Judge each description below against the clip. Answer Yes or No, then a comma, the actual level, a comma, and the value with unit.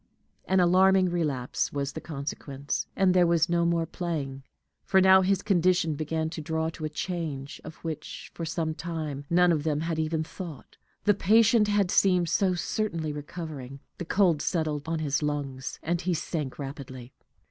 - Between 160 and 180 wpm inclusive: Yes, average, 170 wpm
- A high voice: No, medium, 165 Hz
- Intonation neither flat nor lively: Yes, average, 3.3 semitones